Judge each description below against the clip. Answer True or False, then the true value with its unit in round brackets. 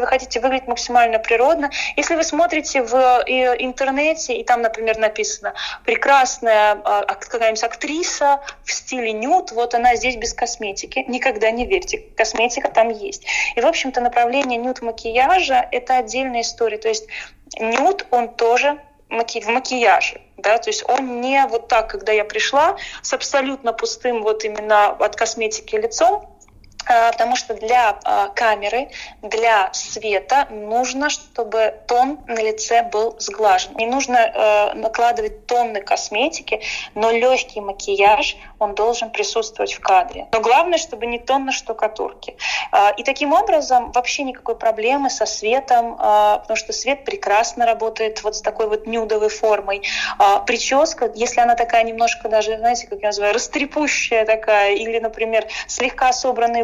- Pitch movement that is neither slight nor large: True (3.7 semitones)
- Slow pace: False (145 wpm)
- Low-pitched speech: False (240 Hz)